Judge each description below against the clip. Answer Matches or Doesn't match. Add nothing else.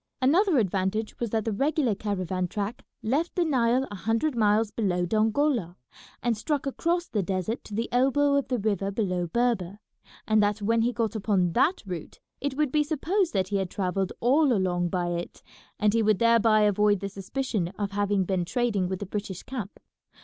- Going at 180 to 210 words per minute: Matches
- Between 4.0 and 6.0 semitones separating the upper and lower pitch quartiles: Matches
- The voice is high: Matches